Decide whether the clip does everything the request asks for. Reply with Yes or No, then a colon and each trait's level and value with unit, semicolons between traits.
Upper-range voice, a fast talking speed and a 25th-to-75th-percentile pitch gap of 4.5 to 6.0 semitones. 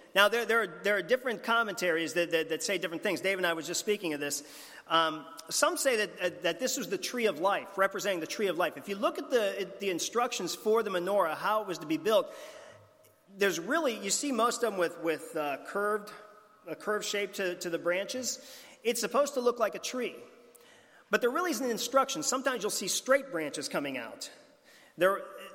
Yes: high, 205 Hz; fast, 225 wpm; wide, 5.6 semitones